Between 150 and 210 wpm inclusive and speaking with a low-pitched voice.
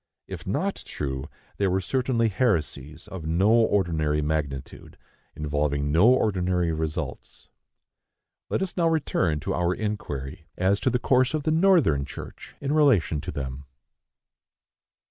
No: slow, 135 wpm; very low, 90 Hz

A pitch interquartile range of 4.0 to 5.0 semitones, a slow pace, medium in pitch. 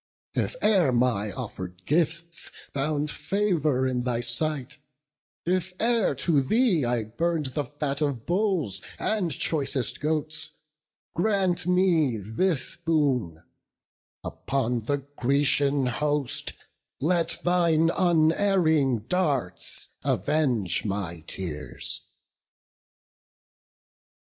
No: wide, 5.5 semitones; slow, 90 wpm; medium, 150 Hz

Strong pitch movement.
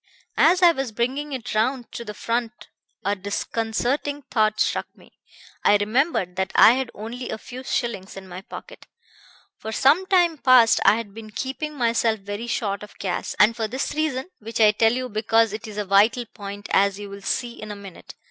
No: average, 3.8 semitones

